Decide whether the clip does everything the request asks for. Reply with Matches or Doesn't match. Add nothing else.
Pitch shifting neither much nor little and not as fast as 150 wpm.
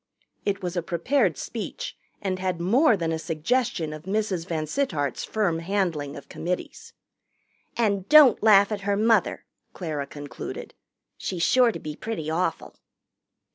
Matches